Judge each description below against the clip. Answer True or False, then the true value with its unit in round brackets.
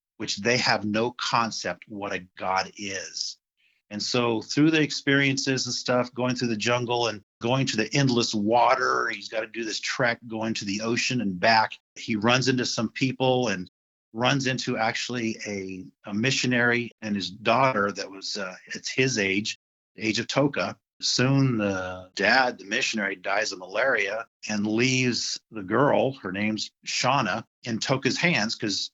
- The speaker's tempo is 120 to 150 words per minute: False (170 wpm)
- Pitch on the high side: False (115 Hz)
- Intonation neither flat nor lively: True (3.3 semitones)